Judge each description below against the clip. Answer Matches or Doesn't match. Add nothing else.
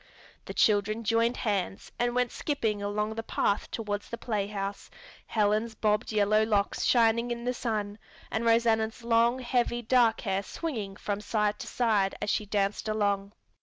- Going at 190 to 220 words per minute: Doesn't match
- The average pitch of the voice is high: Matches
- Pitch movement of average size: Doesn't match